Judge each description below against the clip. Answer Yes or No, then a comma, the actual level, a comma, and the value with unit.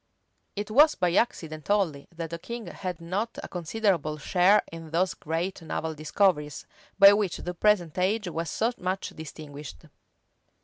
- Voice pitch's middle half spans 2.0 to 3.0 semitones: No, average, 4.2 semitones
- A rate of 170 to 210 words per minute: No, average, 150 wpm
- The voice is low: No, medium, 175 Hz